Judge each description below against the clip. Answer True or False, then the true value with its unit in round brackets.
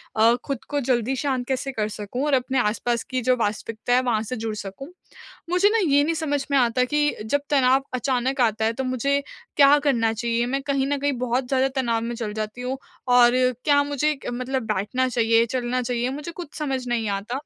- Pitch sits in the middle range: False (255 Hz)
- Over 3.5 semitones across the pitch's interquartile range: False (3.0 semitones)